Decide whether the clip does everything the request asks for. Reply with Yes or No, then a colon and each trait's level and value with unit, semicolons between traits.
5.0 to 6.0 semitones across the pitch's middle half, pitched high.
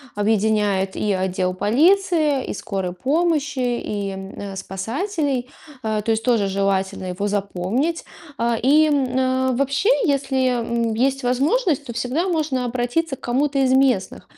Yes: wide, 5.5 semitones; high, 245 Hz